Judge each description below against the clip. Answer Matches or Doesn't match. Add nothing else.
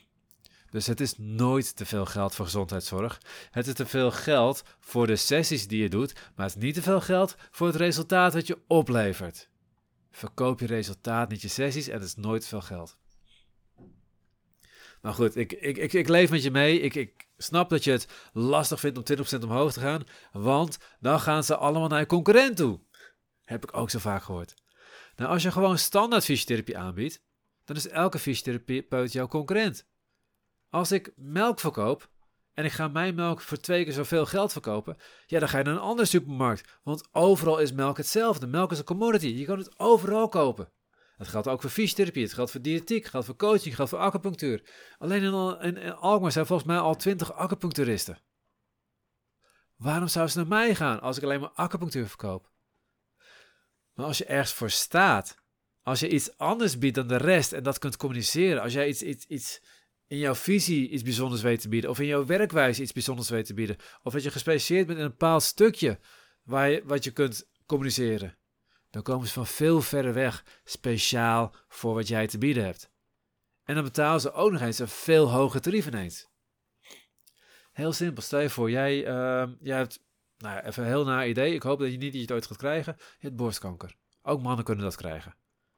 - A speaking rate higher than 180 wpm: Matches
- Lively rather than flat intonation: Matches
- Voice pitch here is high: Doesn't match